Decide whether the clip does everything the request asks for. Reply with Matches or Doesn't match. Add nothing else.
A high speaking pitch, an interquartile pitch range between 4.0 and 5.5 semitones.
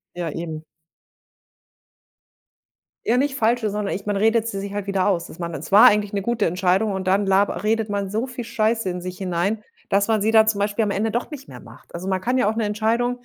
Doesn't match